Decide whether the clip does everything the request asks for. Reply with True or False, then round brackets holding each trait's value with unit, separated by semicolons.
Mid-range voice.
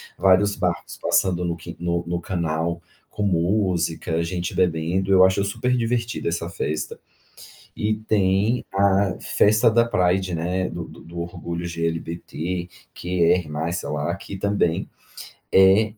False (90 Hz)